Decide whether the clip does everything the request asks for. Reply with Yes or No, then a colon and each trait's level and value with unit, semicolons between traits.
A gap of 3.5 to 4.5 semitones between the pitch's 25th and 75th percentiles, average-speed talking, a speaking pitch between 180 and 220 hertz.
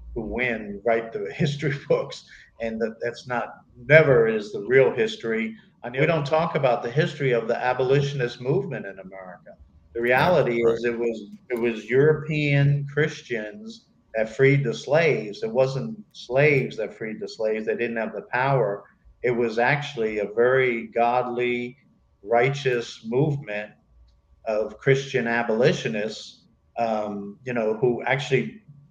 No: average, 4.1 semitones; average, 145 wpm; low, 125 Hz